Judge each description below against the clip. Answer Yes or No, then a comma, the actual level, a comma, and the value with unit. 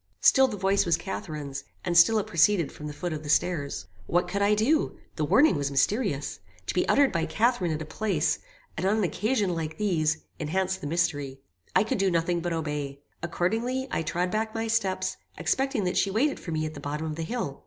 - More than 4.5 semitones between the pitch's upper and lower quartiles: Yes, average, 5.3 semitones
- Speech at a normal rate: No, fast, 215 wpm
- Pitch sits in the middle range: Yes, medium, 175 Hz